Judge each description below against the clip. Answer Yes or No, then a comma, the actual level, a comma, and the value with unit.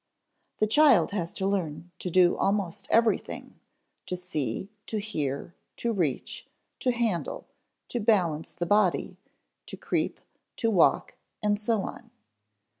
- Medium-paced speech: No, slow, 130 wpm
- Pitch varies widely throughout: No, average, 3.9 semitones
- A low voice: No, high, 195 Hz